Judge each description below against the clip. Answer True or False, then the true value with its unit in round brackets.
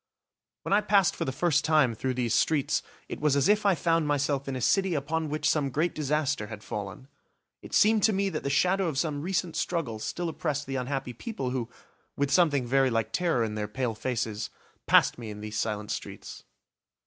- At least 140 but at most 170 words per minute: False (205 wpm)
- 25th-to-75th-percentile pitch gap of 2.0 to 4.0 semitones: False (5.3 semitones)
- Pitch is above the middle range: False (140 Hz)